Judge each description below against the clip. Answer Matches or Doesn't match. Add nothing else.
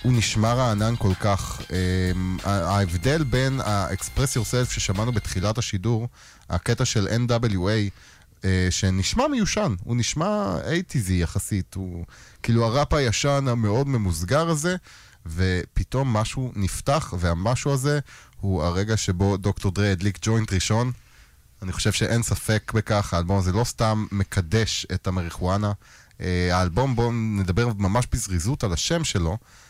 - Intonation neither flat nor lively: Matches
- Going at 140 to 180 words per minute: Doesn't match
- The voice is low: Matches